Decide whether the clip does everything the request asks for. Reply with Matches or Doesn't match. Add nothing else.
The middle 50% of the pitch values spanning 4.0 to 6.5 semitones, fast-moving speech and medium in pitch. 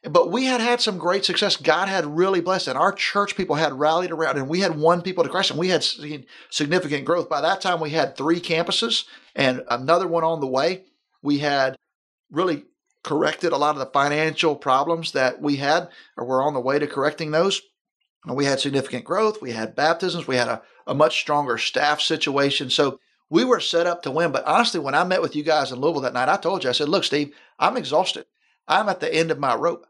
Matches